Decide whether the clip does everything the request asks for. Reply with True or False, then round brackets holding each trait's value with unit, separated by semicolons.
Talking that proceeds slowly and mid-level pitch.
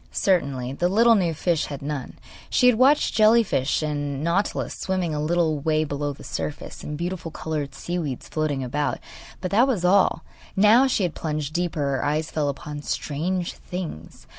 False (180 wpm; 160 Hz)